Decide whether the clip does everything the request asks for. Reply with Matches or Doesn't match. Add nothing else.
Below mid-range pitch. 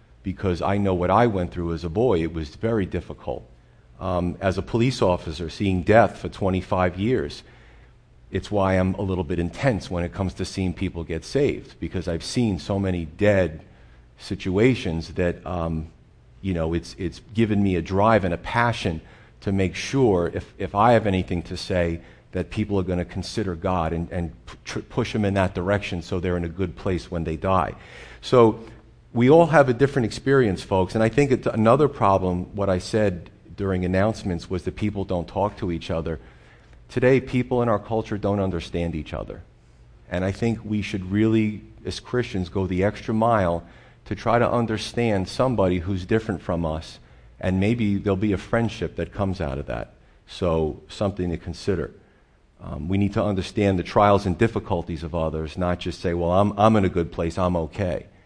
Matches